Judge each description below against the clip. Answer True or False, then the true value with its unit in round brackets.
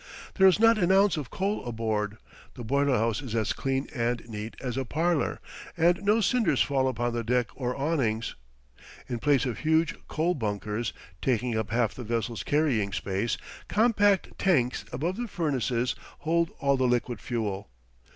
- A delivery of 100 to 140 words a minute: False (170 wpm)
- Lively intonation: True (6.2 semitones)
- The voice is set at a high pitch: False (130 Hz)